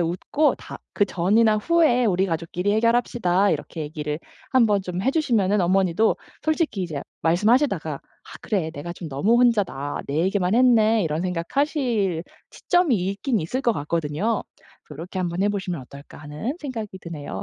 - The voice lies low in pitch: No, high, 190 Hz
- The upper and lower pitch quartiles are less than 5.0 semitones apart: No, wide, 5.6 semitones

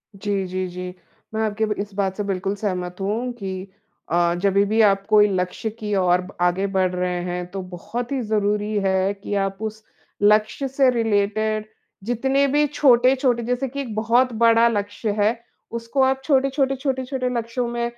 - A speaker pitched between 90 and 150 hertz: No, high, 215 Hz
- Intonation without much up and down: No, average, 3.9 semitones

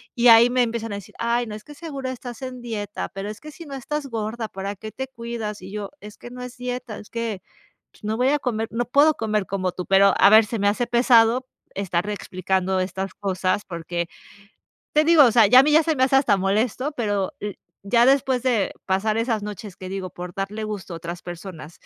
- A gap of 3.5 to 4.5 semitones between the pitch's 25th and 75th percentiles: Yes, average, 4.1 semitones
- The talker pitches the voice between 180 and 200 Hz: No, high, 220 Hz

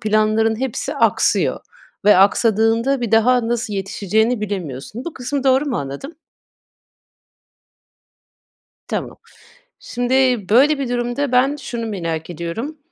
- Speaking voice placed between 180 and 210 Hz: No, high, 230 Hz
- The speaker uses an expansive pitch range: No, average, 3.5 semitones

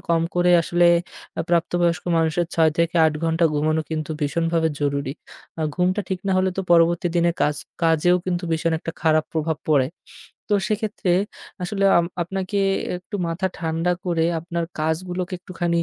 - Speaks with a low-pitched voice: No, medium, 170 Hz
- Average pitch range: No, narrow, 1.8 semitones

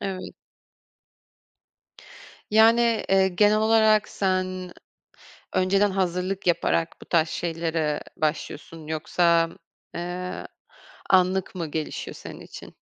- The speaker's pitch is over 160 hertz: Yes, medium, 185 Hz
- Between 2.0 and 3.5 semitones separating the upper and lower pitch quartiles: Yes, average, 2.8 semitones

